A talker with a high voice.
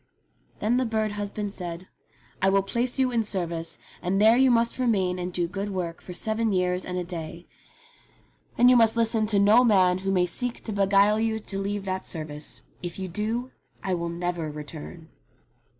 Yes: high, 195 Hz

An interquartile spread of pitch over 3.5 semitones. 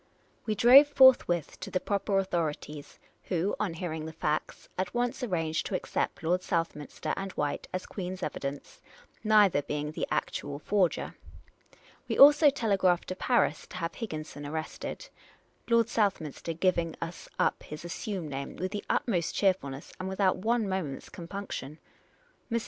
Yes: average, 4.5 semitones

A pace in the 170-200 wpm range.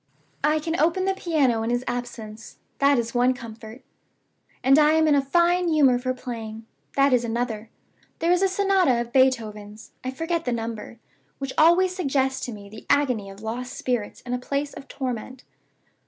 Yes: average, 185 wpm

